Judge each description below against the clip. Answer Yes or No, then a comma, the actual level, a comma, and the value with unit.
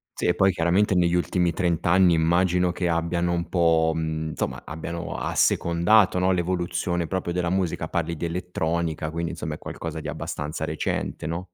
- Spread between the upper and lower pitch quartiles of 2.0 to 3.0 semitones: No, narrow, 1.4 semitones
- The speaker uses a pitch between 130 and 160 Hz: No, very low, 85 Hz